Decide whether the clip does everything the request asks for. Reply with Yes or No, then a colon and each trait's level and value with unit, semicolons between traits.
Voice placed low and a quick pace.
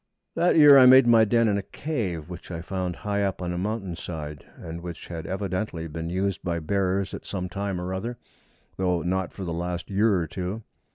Yes: very low, 95 Hz; fast, 215 wpm